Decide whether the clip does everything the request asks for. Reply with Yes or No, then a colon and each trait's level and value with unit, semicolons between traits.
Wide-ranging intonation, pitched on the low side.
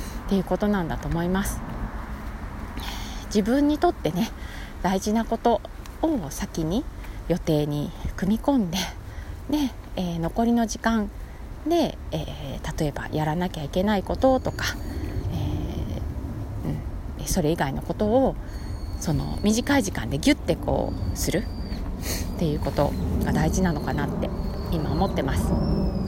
No: wide, 8.3 semitones; high, 190 Hz